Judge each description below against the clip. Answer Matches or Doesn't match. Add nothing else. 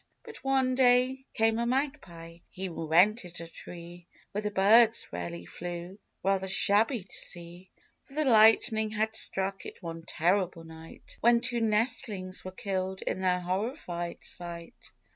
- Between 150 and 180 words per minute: Matches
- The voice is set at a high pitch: Matches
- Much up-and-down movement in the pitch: Doesn't match